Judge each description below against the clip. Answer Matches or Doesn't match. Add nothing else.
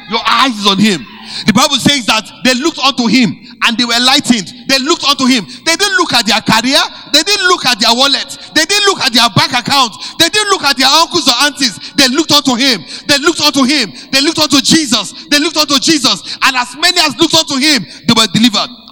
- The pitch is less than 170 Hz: Doesn't match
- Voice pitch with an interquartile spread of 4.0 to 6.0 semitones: Matches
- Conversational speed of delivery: Doesn't match